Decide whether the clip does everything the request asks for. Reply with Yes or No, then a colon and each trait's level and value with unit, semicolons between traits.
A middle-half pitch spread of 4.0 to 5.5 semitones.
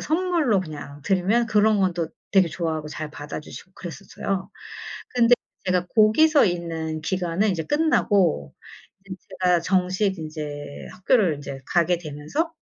Yes: average, 5.1 semitones